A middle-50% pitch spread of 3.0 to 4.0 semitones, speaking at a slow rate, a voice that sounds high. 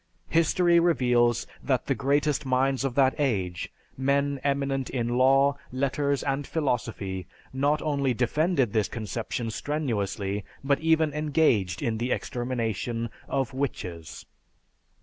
No: average, 3.5 semitones; slow, 120 wpm; low, 130 Hz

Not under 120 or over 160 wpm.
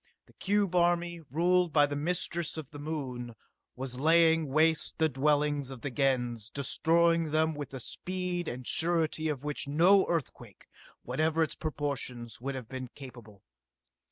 Yes: average, 155 wpm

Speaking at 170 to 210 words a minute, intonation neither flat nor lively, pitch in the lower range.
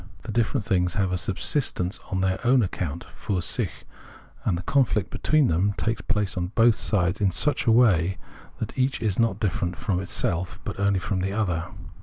Yes: average, 190 wpm; average, 3.8 semitones; low, 100 Hz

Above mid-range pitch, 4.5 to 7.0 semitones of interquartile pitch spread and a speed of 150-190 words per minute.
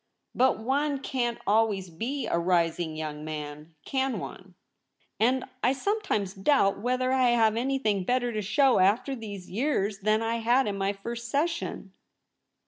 Yes: high, 225 Hz; average, 5.1 semitones; average, 155 wpm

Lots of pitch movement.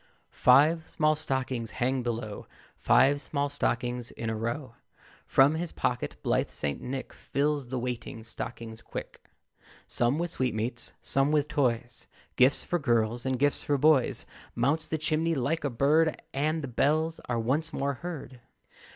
No: average, 4.0 semitones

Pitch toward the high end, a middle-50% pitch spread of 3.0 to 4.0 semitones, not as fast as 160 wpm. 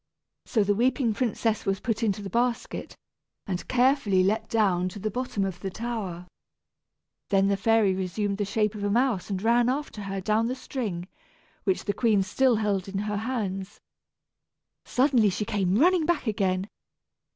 No: high, 210 Hz; average, 3.3 semitones; average, 170 wpm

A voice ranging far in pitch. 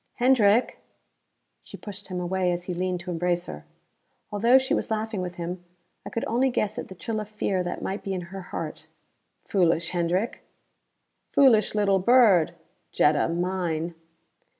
No: average, 3.4 semitones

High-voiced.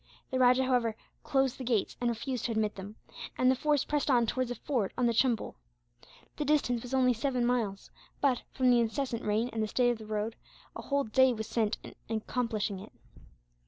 Yes: high, 245 Hz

